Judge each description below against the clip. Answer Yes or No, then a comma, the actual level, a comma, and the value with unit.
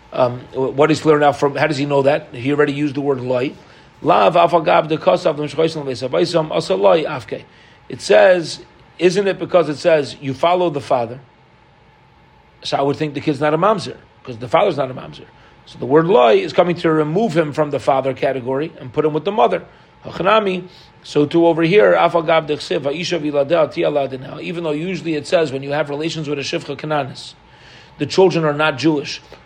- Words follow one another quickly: No, average, 170 wpm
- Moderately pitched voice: Yes, medium, 155 Hz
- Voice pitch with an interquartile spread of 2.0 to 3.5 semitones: Yes, average, 3.1 semitones